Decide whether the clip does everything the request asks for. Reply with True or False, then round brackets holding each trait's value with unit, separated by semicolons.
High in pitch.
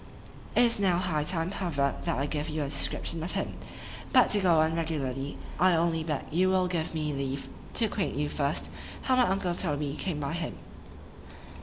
False (165 Hz)